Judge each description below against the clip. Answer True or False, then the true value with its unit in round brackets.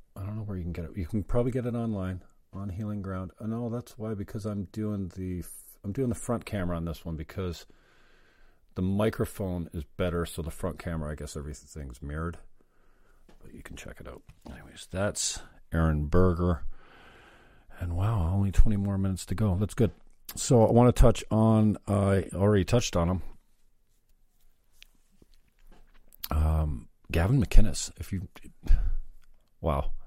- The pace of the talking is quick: False (170 wpm)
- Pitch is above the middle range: False (95 Hz)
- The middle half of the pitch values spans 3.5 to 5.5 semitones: True (4.1 semitones)